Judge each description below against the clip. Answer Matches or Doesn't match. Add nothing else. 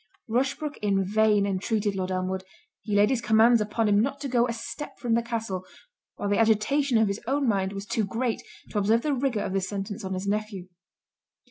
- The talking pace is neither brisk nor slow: Doesn't match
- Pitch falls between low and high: Doesn't match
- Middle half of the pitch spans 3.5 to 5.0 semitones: Doesn't match